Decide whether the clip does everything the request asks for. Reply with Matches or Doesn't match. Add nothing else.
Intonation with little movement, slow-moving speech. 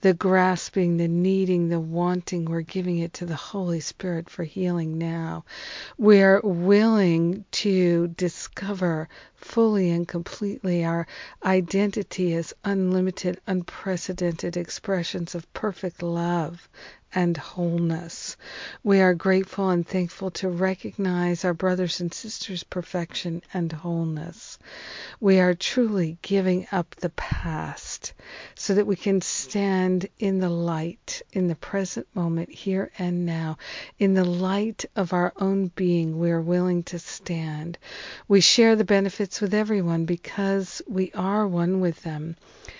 Matches